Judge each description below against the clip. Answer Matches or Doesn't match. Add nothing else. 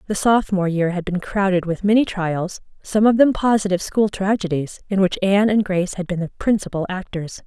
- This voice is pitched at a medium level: Doesn't match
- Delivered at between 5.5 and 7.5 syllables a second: Matches